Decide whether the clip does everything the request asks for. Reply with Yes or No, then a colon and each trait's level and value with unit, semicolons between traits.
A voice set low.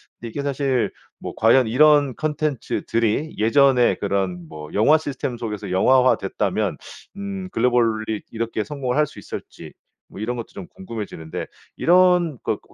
Yes: low, 125 Hz